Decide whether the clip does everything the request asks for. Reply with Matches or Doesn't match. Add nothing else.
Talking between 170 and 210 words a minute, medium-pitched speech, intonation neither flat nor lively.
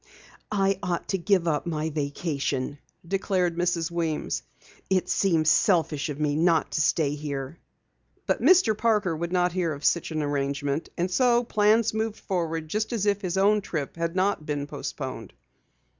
Doesn't match